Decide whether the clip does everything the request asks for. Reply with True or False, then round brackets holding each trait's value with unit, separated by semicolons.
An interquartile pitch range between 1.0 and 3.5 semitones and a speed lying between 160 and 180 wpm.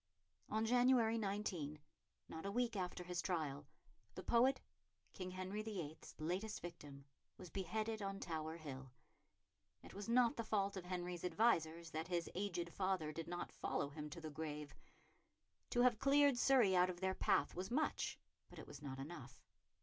False (5.3 semitones; 165 wpm)